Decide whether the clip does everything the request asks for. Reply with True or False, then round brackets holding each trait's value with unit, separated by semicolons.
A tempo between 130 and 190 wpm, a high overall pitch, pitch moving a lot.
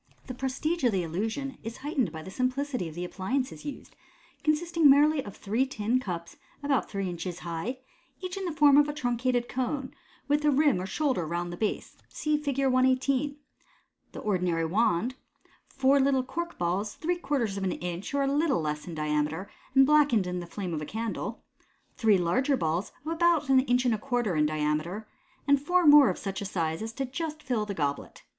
False (200 wpm; 245 Hz; 7.7 semitones)